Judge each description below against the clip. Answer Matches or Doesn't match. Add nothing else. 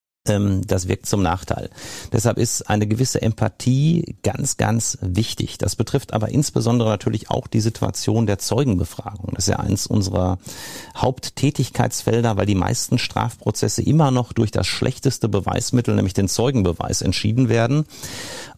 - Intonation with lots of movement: Doesn't match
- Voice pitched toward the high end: Doesn't match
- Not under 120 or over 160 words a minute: Matches